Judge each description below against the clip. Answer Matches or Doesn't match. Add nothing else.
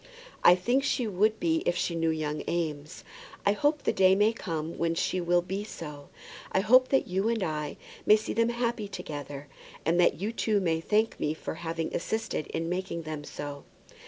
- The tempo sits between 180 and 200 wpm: Matches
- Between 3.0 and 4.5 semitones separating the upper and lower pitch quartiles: Doesn't match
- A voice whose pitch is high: Doesn't match